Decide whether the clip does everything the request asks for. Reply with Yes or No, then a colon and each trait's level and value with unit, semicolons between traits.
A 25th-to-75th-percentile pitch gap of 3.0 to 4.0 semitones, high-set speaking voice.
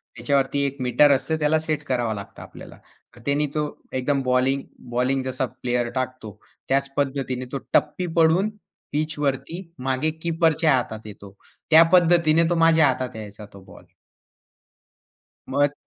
No: average, 3.4 semitones; low, 135 Hz